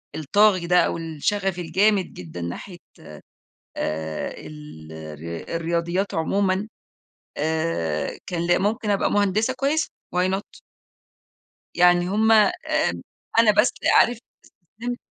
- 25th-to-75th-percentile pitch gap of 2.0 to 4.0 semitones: No, average, 4.9 semitones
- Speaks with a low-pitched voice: No, medium, 180 Hz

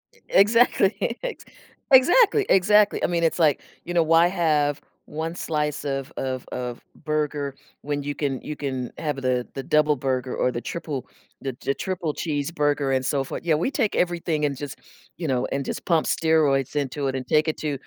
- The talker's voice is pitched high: No, medium, 150 Hz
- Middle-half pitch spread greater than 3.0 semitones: Yes, average, 3.5 semitones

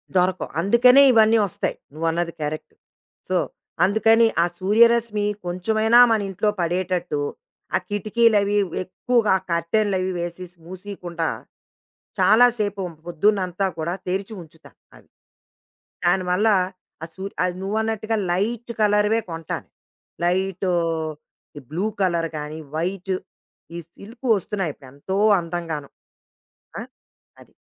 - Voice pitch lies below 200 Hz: Yes, high, 190 Hz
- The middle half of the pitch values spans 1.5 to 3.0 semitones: No, average, 3.7 semitones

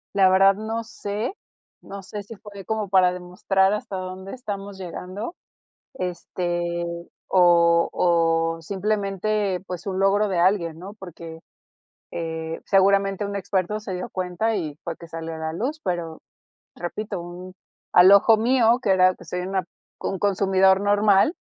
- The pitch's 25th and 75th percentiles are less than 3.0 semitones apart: Yes, narrow, 2.6 semitones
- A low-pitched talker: No, high, 190 Hz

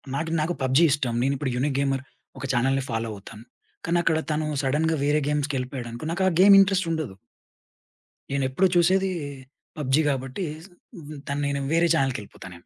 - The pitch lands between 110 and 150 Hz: Yes, medium, 140 Hz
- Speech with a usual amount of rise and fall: Yes, average, 3.7 semitones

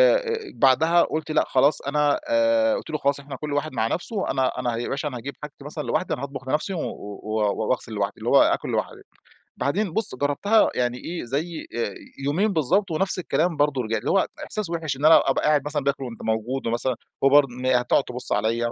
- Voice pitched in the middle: Yes, medium, 145 Hz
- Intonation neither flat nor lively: Yes, average, 4.7 semitones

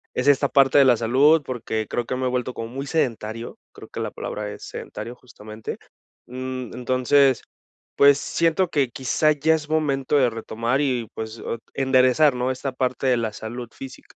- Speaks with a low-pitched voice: Yes, low, 130 Hz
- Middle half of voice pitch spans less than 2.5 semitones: No, average, 2.8 semitones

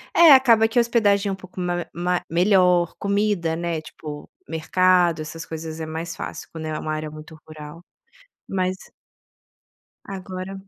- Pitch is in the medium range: Yes, medium, 175 Hz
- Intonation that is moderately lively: Yes, average, 3.4 semitones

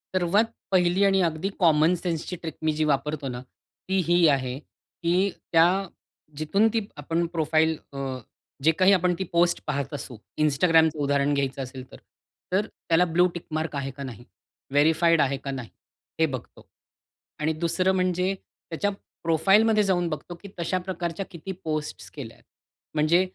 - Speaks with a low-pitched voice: No, medium, 165 Hz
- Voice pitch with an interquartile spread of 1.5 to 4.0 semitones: Yes, average, 3.7 semitones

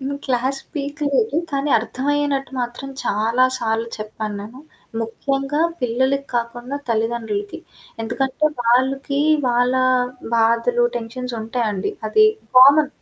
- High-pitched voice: Yes, high, 245 Hz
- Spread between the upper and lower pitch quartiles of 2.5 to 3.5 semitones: Yes, average, 3.2 semitones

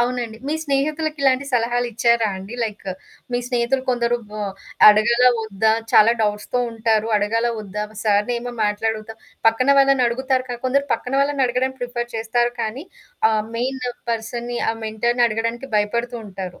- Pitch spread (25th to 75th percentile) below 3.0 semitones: Yes, narrow, 2.4 semitones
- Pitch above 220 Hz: Yes, high, 235 Hz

